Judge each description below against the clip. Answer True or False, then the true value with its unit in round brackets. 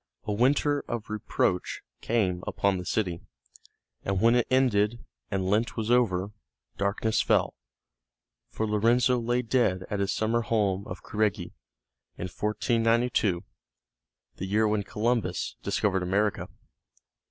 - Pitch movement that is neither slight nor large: True (3.2 semitones)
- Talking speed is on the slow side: True (125 wpm)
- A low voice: True (105 Hz)